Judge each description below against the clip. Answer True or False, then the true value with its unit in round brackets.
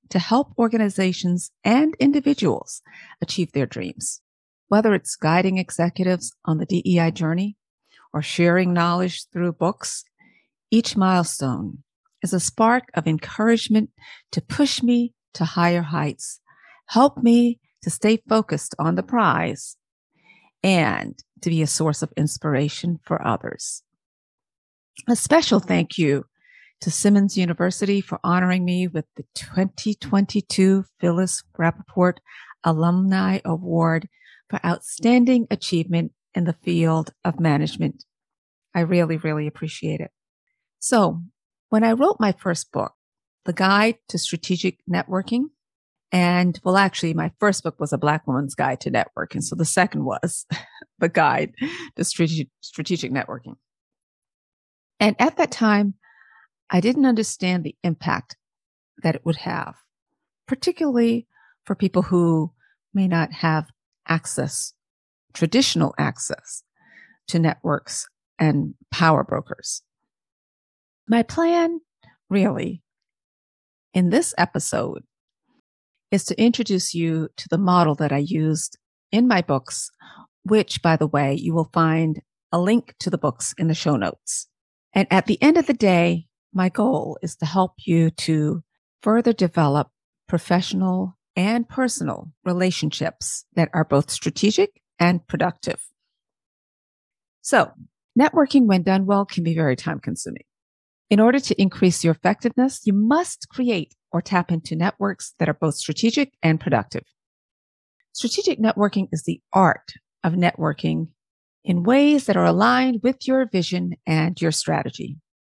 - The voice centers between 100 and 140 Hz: False (180 Hz)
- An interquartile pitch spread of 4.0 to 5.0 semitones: True (4.6 semitones)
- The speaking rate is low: True (130 wpm)